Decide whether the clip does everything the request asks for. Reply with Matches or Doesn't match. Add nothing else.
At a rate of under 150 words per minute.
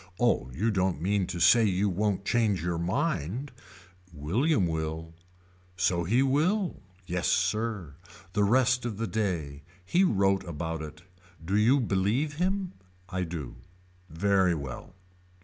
Matches